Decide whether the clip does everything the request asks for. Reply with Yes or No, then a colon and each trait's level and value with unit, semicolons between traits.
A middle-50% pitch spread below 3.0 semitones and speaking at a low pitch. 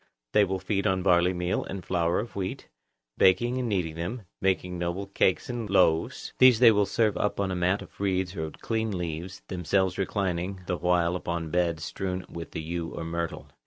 Yes: narrow, 2.5 semitones; very low, 90 Hz